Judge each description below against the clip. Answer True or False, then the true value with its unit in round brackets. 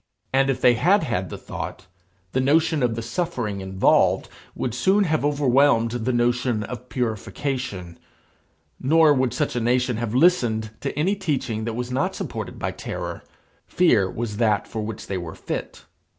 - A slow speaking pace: False (165 wpm)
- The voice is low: True (125 Hz)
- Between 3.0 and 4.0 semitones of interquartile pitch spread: False (4.4 semitones)